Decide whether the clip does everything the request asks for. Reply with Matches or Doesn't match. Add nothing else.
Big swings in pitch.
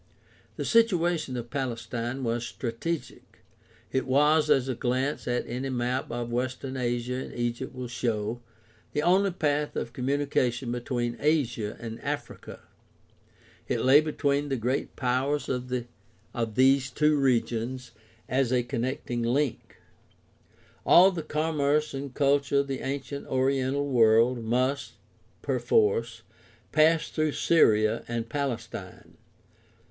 Doesn't match